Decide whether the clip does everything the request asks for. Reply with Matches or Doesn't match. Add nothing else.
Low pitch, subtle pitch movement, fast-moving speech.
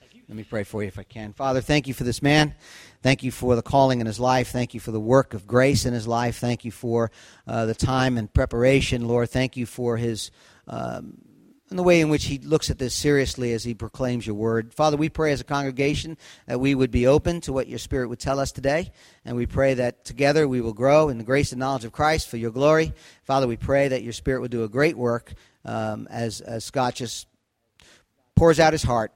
Doesn't match